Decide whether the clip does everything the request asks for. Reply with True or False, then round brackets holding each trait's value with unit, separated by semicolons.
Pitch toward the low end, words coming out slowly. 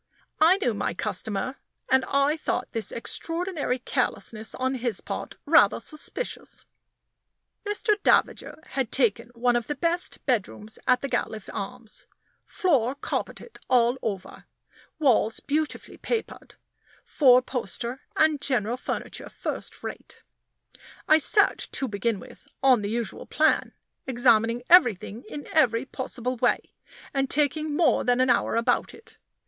False (255 Hz; 130 wpm)